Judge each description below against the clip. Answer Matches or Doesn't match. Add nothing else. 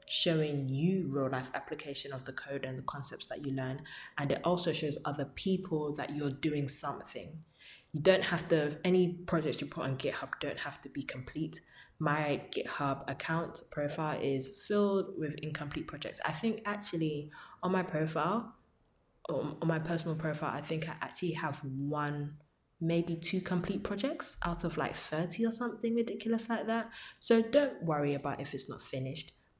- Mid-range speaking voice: Matches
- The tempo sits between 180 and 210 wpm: Doesn't match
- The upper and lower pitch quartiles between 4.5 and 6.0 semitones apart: Doesn't match